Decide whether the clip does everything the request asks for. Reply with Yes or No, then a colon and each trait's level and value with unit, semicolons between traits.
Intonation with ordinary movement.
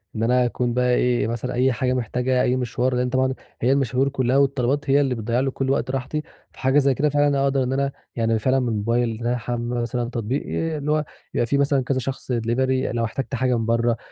No: narrow, 2.1 semitones